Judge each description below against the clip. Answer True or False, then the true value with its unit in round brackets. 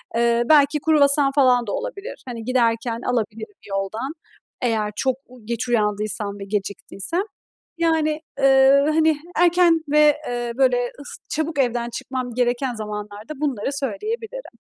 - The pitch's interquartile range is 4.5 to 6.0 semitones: True (4.8 semitones)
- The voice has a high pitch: True (255 Hz)